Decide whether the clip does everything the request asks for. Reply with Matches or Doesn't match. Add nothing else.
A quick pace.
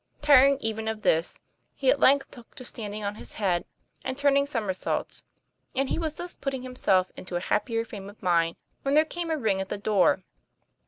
Matches